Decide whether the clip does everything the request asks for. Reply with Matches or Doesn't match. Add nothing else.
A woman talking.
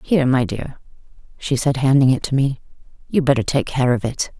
Matches